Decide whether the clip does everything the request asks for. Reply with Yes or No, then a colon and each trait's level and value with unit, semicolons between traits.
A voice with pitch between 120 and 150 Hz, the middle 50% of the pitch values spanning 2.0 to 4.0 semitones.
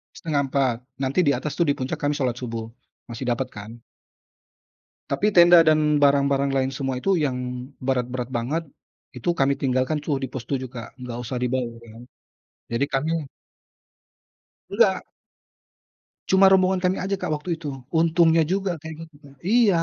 No: medium, 140 Hz; average, 4.6 semitones